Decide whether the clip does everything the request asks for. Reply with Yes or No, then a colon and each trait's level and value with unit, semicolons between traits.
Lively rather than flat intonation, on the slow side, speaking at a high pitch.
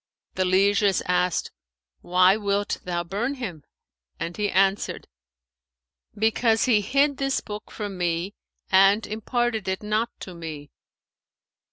No: average, 3.4 semitones; slow, 125 wpm; high, 200 Hz